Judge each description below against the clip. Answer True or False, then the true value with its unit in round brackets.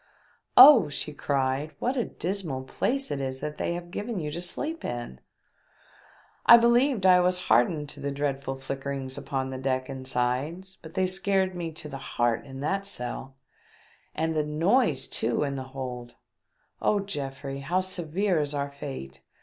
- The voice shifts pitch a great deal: True (5.8 semitones)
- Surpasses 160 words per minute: True (170 wpm)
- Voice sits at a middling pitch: True (150 Hz)